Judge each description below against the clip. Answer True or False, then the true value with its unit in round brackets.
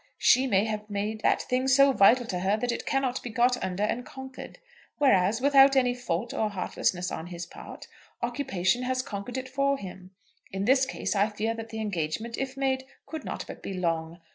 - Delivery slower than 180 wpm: False (200 wpm)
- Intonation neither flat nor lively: True (4.9 semitones)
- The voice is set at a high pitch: True (230 Hz)